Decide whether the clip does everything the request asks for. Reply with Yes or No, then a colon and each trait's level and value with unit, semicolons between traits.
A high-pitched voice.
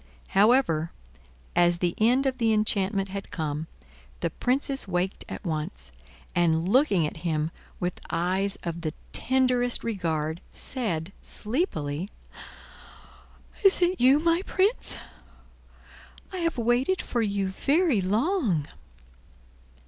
Yes: high, 200 Hz